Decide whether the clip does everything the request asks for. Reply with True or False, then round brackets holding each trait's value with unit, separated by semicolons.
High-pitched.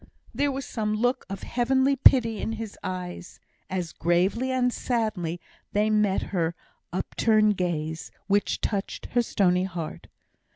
True (210 Hz)